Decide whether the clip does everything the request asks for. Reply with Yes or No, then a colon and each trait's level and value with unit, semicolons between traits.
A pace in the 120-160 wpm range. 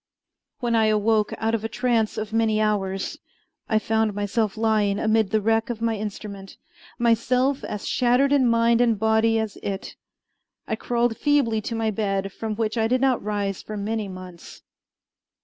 No: average, 170 wpm